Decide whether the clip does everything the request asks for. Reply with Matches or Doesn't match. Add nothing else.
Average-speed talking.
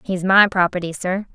Matches